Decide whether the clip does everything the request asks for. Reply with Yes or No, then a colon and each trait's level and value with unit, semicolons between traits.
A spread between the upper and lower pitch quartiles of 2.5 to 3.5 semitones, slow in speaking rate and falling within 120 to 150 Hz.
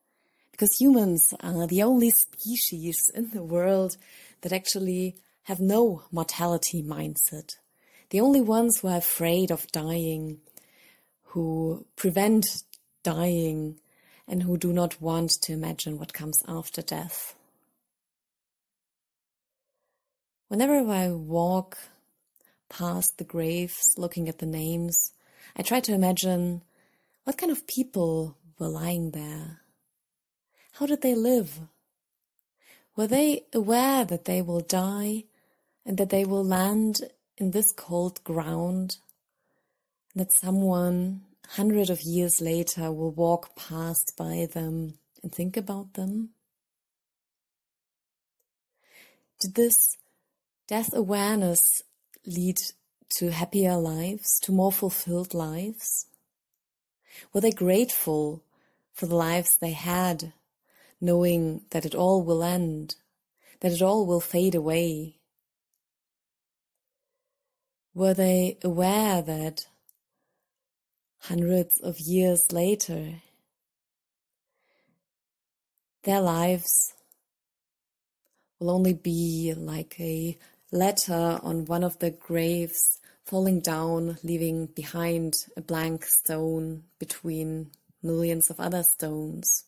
No: average, 3.2 semitones; slow, 105 wpm; medium, 175 Hz